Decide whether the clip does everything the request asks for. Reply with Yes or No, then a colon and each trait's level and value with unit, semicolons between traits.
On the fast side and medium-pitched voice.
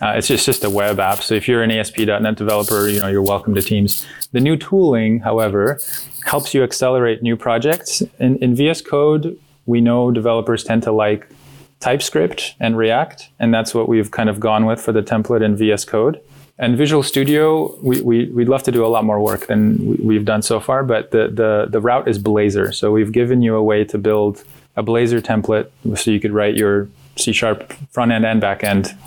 No: fast, 215 wpm; low, 115 Hz